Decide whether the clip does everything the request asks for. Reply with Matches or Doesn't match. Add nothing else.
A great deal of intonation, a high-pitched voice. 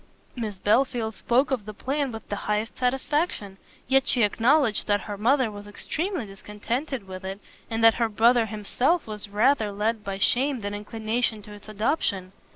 Doesn't match